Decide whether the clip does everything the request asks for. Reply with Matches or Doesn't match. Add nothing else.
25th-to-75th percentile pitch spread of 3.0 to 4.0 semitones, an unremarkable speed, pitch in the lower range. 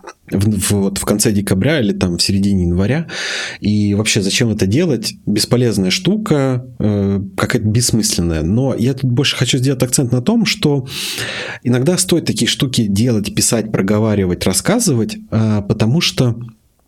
Doesn't match